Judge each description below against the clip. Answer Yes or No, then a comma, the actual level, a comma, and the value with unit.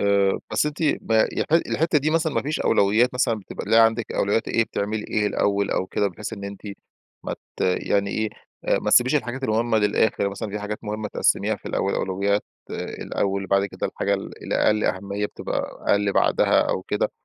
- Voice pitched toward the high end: No, low, 105 Hz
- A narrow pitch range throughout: Yes, narrow, 2.3 semitones